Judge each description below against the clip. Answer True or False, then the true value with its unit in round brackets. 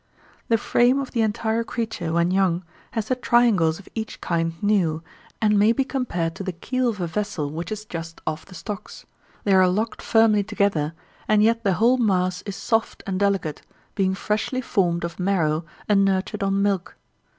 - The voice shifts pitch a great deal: False (4.2 semitones)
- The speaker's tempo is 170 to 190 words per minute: True (185 wpm)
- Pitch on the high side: True (200 Hz)